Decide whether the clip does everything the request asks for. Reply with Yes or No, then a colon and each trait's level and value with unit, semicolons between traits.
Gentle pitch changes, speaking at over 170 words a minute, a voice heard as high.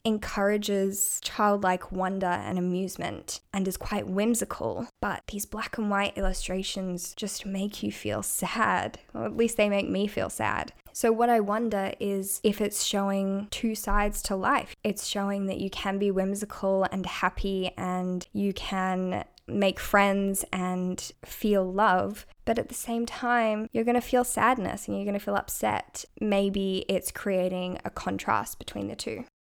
No: narrow, 1.9 semitones; average, 165 wpm; high, 195 Hz